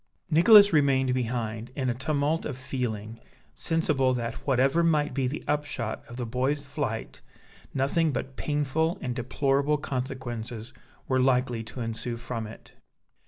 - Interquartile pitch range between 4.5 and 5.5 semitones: No, average, 3.3 semitones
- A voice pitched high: No, low, 130 Hz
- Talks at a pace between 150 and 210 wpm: No, average, 140 wpm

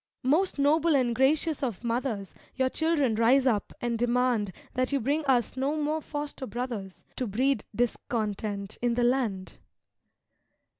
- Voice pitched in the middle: No, very high, 250 Hz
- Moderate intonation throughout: Yes, average, 3.4 semitones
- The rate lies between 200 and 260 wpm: No, average, 145 wpm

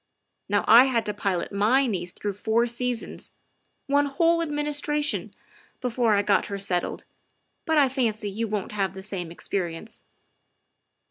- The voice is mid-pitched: No, high, 225 Hz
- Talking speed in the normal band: Yes, average, 150 wpm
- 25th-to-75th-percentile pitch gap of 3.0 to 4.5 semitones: No, average, 5.2 semitones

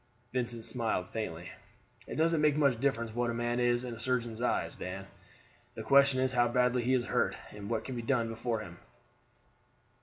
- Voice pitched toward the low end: Yes, low, 120 Hz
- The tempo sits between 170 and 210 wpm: Yes, average, 190 wpm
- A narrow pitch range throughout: Yes, narrow, 2.2 semitones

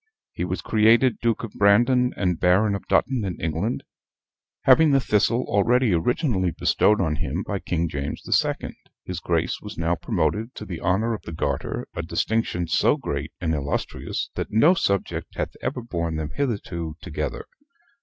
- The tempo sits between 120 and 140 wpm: No, average, 170 wpm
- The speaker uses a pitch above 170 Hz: No, low, 100 Hz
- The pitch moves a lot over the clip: Yes, wide, 5.7 semitones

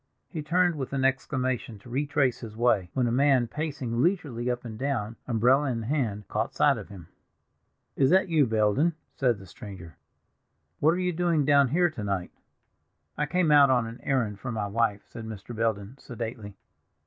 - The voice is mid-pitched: No, low, 125 Hz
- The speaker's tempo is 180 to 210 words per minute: Yes, average, 185 wpm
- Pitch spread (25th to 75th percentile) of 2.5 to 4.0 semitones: No, average, 4.8 semitones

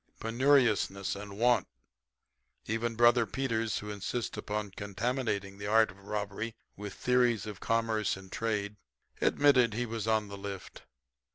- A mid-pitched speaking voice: No, low, 110 Hz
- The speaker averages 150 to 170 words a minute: No, average, 140 wpm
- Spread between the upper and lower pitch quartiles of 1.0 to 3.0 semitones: Yes, narrow, 2.6 semitones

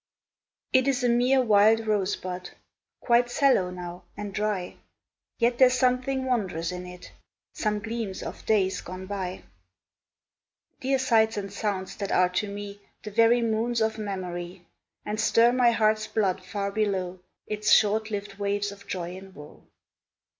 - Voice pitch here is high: Yes, high, 210 Hz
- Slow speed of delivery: No, average, 155 wpm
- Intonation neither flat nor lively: Yes, average, 3.5 semitones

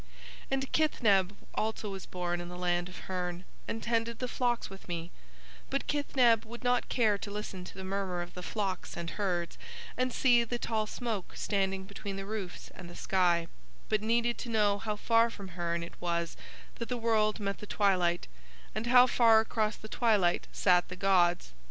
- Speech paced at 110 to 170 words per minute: No, average, 190 wpm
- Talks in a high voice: Yes, high, 200 Hz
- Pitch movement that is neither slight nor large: Yes, average, 4.1 semitones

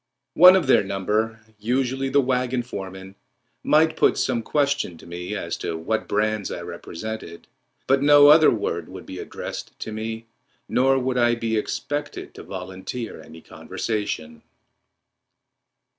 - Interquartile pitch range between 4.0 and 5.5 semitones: Yes, average, 4.9 semitones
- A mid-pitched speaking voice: No, low, 115 Hz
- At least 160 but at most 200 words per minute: No, average, 145 wpm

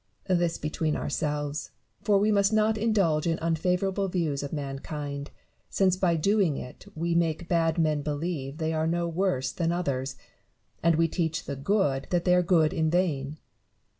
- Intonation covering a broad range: No, average, 3.3 semitones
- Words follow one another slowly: No, average, 170 wpm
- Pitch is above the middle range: No, medium, 165 Hz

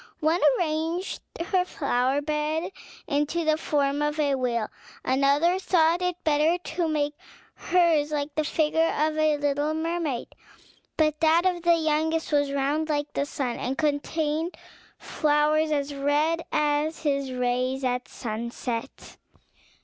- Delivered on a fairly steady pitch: Yes, narrow, 2.2 semitones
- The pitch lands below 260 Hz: No, very high, 300 Hz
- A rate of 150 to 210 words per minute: No, slow, 135 wpm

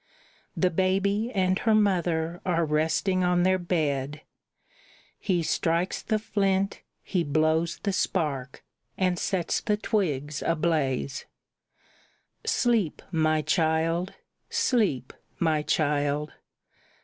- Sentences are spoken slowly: Yes, slow, 100 wpm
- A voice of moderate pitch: Yes, medium, 170 Hz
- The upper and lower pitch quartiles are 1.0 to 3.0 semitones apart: No, average, 3.6 semitones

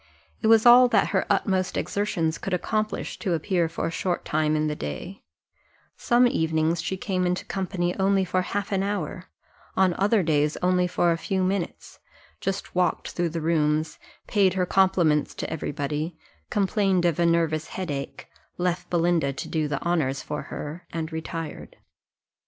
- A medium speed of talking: Yes, average, 170 wpm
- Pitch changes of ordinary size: Yes, average, 3.2 semitones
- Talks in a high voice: No, medium, 175 Hz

